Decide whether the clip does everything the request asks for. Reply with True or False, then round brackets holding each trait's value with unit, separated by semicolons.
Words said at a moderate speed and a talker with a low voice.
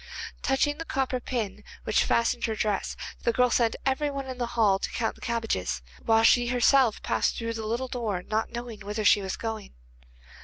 False (195 wpm; 230 Hz)